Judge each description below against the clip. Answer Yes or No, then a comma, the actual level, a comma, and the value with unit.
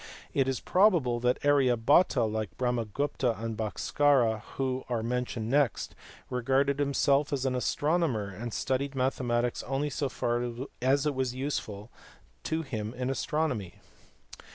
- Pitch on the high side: No, low, 130 Hz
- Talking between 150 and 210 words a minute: No, average, 140 wpm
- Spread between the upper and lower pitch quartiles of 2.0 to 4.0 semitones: Yes, average, 3.0 semitones